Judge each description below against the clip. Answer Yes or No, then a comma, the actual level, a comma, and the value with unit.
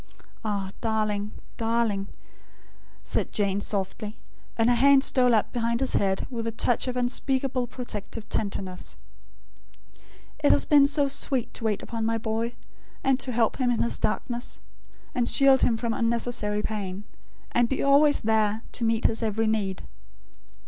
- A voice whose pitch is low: No, high, 230 Hz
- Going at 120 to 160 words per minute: Yes, average, 150 wpm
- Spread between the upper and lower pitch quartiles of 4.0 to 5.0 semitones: No, average, 2.7 semitones